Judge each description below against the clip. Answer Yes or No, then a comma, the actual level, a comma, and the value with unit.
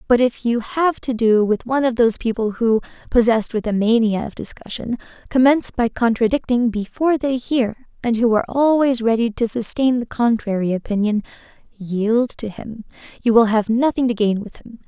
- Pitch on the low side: No, high, 230 Hz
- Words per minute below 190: Yes, average, 180 wpm